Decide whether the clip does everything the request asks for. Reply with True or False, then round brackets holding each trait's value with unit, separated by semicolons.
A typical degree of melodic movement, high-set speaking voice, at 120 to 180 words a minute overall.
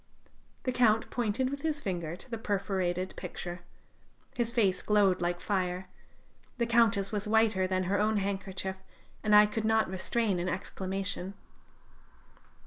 True (3.0 semitones; 200 Hz; 140 wpm)